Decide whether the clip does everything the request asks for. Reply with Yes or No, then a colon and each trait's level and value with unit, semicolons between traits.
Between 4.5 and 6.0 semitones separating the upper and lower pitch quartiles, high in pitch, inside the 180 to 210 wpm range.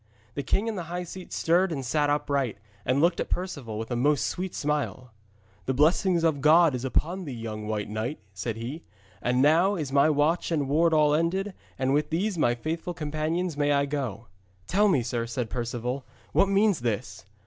No: average, 5.2 semitones; medium, 145 Hz; average, 195 wpm